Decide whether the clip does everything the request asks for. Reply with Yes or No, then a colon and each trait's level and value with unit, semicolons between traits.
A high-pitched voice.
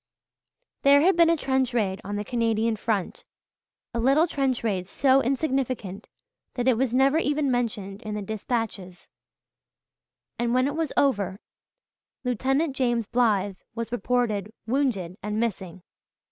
Yes: high, 235 Hz